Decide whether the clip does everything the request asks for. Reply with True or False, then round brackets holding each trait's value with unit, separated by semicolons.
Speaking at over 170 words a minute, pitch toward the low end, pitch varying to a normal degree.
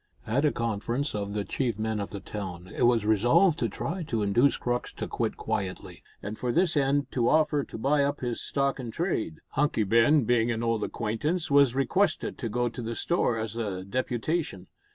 True (200 wpm; 120 Hz; 4.6 semitones)